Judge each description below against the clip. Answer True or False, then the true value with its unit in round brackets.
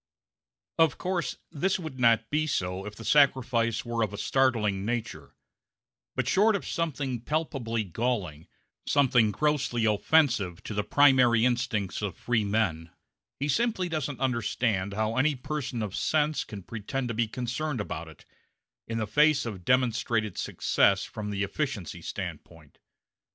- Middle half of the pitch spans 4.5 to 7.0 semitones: True (5.2 semitones)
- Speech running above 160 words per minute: False (145 wpm)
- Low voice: True (120 Hz)